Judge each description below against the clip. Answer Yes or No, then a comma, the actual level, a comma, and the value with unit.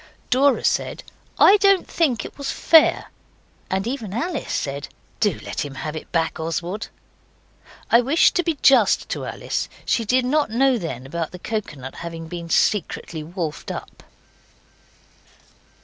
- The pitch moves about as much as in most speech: No, wide, 8.5 semitones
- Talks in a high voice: Yes, high, 210 Hz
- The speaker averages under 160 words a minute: Yes, average, 150 wpm